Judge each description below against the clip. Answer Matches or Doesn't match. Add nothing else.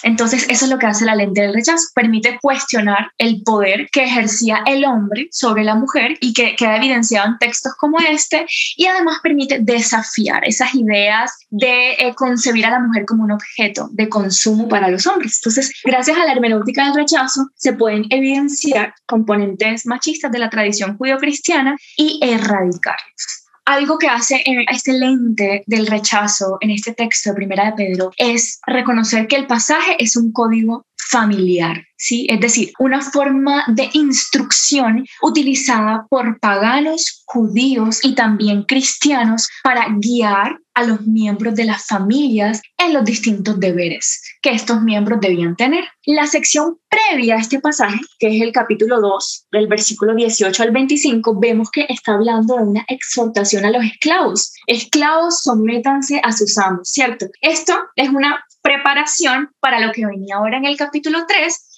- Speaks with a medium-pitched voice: Doesn't match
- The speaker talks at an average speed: Matches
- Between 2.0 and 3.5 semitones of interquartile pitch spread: Doesn't match